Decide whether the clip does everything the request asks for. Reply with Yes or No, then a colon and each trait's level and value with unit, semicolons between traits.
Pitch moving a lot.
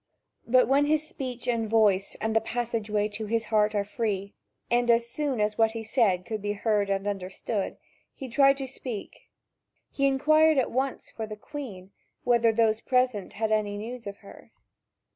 No: average, 3.3 semitones